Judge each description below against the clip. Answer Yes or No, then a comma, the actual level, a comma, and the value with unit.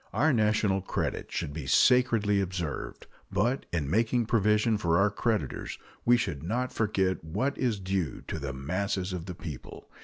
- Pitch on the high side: No, low, 100 Hz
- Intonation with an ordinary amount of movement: Yes, average, 4.7 semitones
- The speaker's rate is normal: Yes, average, 160 wpm